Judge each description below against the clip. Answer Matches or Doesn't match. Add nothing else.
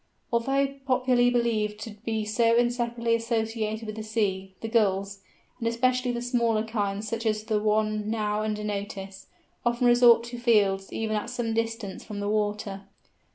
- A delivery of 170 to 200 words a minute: Doesn't match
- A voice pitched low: Doesn't match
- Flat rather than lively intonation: Matches